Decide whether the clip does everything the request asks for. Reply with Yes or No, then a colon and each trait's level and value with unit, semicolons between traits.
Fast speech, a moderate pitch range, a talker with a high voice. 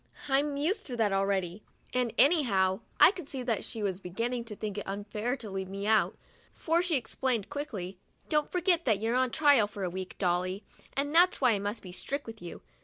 No: fast, 220 wpm; wide, 6.3 semitones; high, 225 Hz